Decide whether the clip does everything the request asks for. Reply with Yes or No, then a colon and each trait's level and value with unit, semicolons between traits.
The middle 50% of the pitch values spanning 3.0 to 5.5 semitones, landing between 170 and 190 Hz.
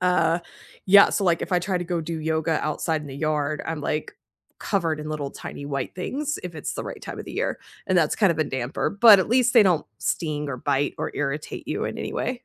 No: average, 3.7 semitones; medium, 160 Hz